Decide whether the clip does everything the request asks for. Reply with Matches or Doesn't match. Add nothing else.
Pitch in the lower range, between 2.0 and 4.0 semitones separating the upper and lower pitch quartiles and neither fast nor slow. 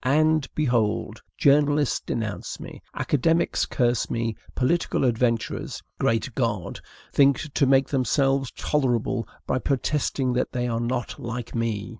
Doesn't match